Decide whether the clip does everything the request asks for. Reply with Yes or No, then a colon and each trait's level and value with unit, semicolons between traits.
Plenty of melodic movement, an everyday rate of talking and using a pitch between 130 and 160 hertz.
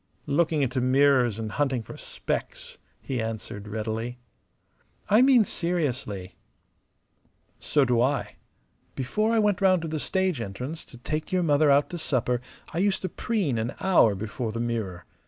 Yes: wide, 6.7 semitones; average, 155 wpm; low, 135 Hz